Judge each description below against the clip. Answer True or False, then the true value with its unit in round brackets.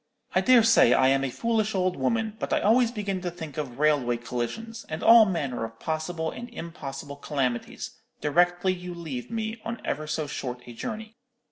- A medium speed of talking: True (190 wpm)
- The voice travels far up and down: True (8.0 semitones)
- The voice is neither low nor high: True (170 Hz)